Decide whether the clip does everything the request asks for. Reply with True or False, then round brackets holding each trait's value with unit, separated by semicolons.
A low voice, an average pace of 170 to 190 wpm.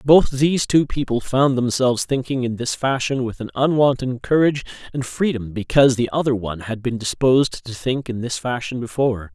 True (125 Hz; 185 wpm)